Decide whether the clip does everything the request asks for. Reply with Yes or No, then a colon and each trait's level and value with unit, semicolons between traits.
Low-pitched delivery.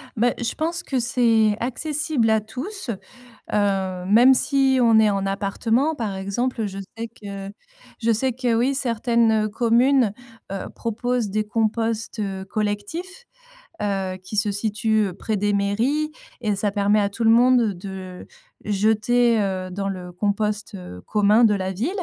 No: high, 220 Hz